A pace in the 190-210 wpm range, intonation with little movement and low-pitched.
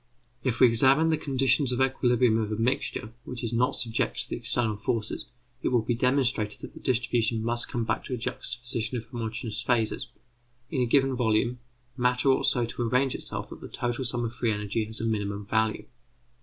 Yes: average, 195 wpm; narrow, 2.1 semitones; low, 120 Hz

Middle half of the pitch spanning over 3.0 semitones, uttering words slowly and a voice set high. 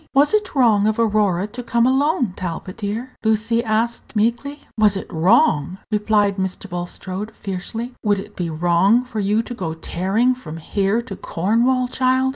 No: average, 4.1 semitones; average, 165 wpm; high, 215 Hz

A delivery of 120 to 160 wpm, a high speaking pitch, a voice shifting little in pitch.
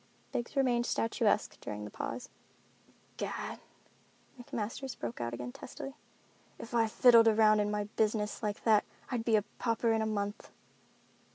Yes: average, 150 wpm; high, 220 Hz; narrow, 2.2 semitones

